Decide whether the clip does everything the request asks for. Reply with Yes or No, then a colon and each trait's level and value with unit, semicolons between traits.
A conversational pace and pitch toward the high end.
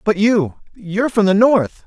Yes: average, 160 wpm; high, 205 Hz